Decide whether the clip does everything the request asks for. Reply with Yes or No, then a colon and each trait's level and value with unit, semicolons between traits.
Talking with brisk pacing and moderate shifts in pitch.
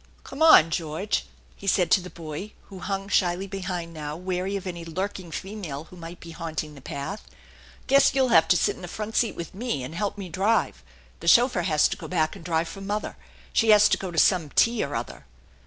Yes: fast, 225 wpm; average, 3.6 semitones